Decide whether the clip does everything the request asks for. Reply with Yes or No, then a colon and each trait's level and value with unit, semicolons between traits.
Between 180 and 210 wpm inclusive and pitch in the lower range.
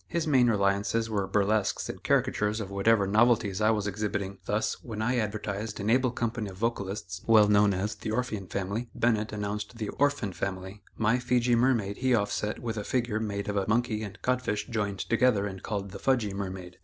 Yes: average, 195 wpm; low, 105 Hz